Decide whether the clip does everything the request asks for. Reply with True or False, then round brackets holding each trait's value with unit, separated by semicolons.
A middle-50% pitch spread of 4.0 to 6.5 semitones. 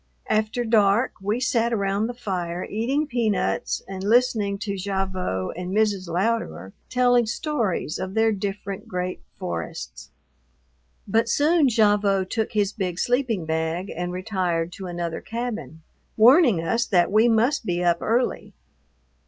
True (4.4 semitones)